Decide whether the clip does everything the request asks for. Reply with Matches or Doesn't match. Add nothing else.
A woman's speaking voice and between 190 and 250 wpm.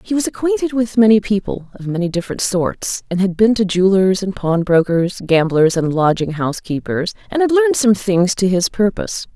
Matches